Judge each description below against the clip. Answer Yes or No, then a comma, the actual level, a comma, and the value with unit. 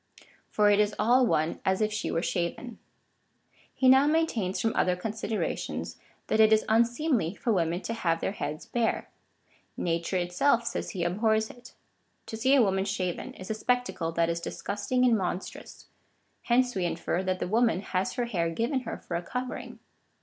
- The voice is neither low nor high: No, high, 215 Hz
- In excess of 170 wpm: Yes, average, 180 wpm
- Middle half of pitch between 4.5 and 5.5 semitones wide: Yes, average, 4.9 semitones